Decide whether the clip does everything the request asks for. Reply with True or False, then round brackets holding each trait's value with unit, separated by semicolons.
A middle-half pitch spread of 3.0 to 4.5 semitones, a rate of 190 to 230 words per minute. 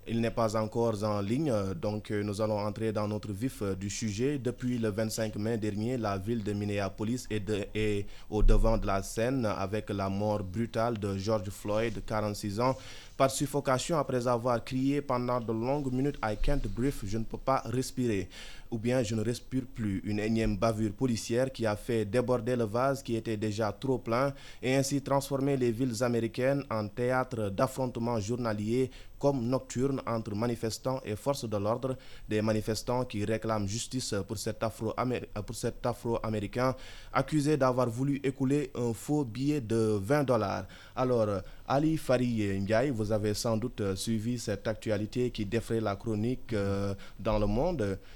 False (3.3 semitones; 170 wpm)